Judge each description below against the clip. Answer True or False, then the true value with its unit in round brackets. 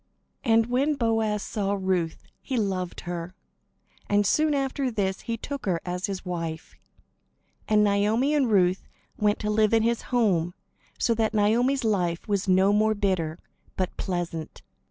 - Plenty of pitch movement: False (3.7 semitones)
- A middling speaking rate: True (155 wpm)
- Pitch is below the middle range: False (205 Hz)